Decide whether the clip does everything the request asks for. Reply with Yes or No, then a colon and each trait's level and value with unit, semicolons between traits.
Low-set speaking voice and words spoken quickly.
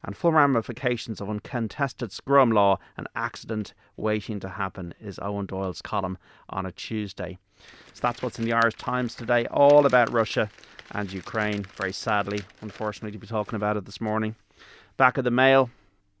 No: low, 110 Hz; average, 170 wpm